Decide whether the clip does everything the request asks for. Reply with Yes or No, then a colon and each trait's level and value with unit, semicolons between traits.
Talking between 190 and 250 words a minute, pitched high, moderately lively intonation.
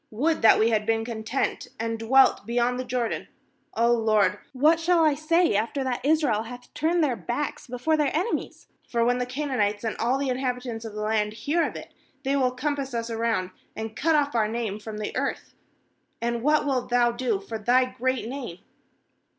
Yes: average, 195 wpm; high, 245 Hz; average, 3.6 semitones